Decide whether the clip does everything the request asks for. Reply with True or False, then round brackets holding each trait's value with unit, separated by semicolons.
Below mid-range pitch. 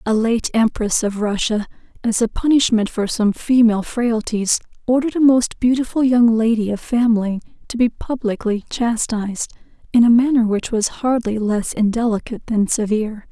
False (225 Hz)